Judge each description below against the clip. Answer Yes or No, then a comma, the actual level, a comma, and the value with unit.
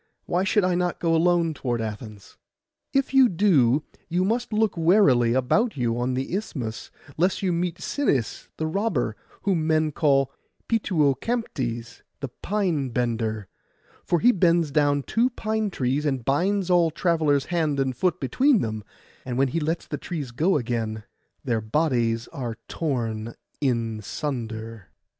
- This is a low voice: No, medium, 150 Hz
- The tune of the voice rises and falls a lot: Yes, wide, 6.9 semitones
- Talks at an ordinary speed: Yes, average, 150 wpm